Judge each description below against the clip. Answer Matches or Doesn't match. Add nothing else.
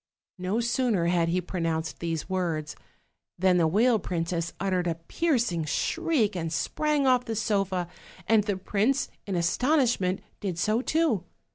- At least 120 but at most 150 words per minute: Matches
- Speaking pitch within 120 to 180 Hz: Doesn't match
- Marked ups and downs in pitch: Matches